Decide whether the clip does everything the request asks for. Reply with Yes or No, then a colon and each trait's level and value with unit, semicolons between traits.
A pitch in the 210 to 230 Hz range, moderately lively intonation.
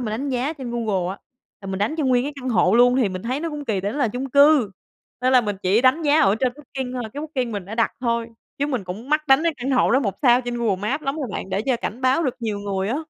No: high, 245 Hz; average, 4.5 semitones